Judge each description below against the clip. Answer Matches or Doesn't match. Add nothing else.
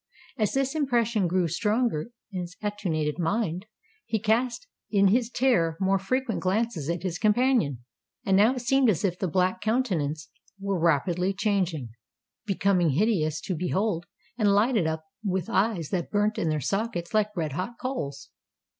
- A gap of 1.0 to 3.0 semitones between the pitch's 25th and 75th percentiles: Doesn't match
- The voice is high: Matches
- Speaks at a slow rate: Doesn't match